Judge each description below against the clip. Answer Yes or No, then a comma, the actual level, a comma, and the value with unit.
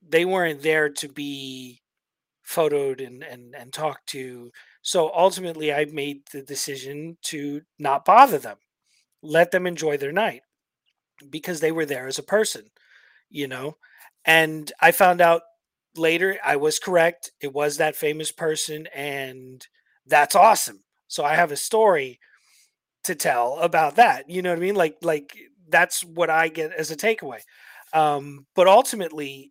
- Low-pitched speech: No, medium, 155 Hz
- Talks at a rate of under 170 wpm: Yes, average, 155 wpm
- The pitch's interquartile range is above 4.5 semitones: No, average, 3.2 semitones